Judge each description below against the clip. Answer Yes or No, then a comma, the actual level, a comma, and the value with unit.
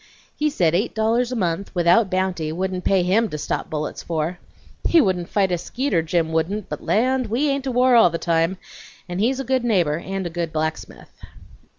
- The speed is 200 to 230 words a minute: Yes, fast, 205 wpm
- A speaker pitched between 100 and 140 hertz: No, high, 190 Hz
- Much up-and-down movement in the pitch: Yes, wide, 5.7 semitones